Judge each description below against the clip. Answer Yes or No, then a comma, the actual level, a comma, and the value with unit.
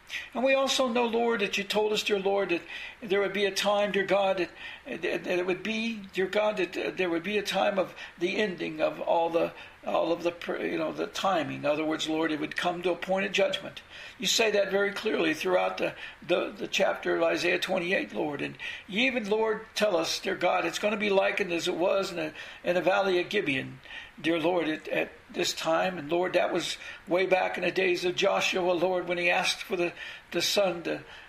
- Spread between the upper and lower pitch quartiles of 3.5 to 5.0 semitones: No, average, 3.0 semitones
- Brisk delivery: Yes, fast, 230 wpm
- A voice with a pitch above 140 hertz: Yes, high, 190 Hz